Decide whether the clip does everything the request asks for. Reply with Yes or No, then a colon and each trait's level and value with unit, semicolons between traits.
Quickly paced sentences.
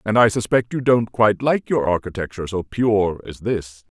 No: average, 195 wpm